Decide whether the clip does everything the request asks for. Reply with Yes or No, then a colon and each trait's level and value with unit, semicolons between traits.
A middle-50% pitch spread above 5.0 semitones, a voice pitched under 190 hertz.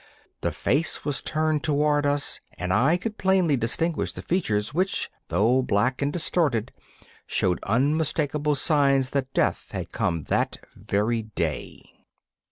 Yes: wide, 5.4 semitones; medium, 140 Hz